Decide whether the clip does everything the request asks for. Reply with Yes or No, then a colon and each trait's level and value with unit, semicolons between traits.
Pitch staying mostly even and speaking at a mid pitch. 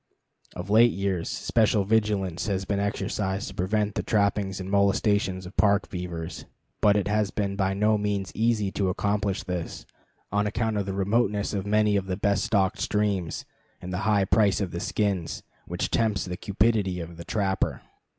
No: narrow, 1.8 semitones; low, 100 Hz